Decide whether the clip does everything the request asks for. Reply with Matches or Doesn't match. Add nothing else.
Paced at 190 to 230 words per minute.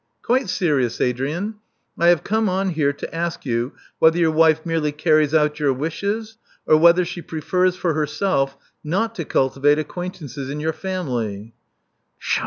Doesn't match